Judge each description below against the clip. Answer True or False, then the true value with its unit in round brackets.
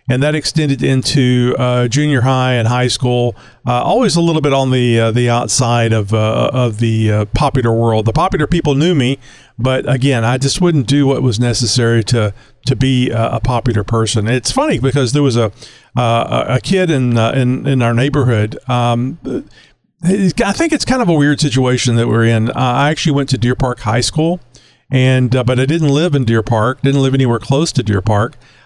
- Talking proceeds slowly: False (205 wpm)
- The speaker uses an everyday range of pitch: True (3.1 semitones)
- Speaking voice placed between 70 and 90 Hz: False (130 Hz)